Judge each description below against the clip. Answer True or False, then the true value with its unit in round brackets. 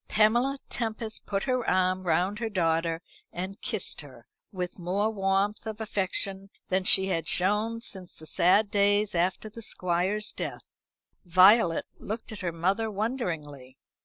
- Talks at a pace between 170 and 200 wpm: False (145 wpm)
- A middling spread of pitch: True (3.4 semitones)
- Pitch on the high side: True (195 Hz)